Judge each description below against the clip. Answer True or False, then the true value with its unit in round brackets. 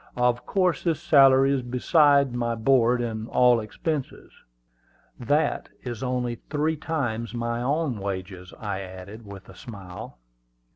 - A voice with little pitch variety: False (4.1 semitones)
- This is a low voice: True (120 Hz)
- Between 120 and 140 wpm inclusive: True (135 wpm)